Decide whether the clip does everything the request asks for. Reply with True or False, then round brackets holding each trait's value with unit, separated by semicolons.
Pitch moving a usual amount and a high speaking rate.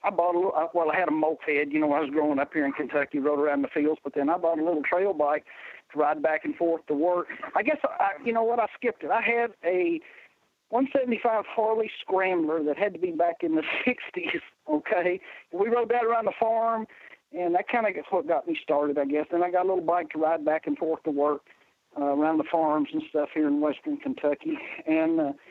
False (7.3 semitones; 245 wpm)